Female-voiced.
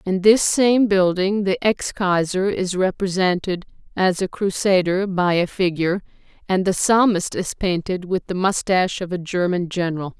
Yes: female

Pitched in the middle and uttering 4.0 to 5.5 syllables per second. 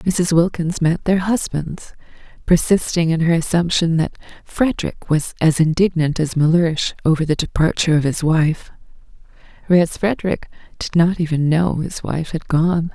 Yes: medium, 165 Hz; 4.8 syllables/s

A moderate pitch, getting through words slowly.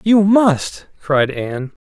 Yes: medium, 170 Hz; slow, 130 wpm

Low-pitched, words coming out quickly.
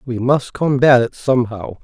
No: low, 125 Hz; average, 165 wpm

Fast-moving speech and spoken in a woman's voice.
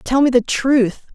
Yes: fast, 210 wpm; female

